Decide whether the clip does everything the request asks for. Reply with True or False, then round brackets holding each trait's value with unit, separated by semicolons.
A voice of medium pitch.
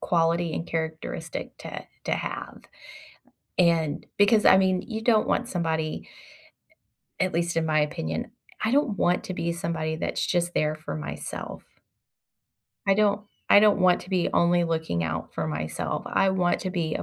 True (170 Hz)